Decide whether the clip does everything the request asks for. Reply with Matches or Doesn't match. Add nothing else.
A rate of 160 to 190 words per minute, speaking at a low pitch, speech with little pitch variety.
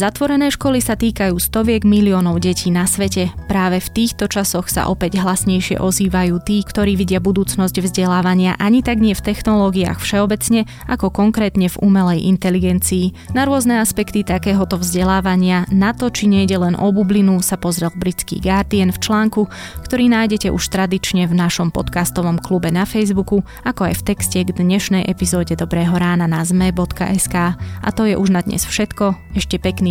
Doesn't match